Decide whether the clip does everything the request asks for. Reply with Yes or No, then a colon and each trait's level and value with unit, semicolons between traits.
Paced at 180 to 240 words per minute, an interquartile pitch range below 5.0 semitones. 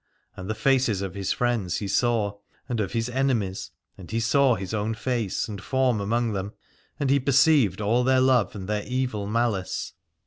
Yes: average, 185 wpm; average, 3.8 semitones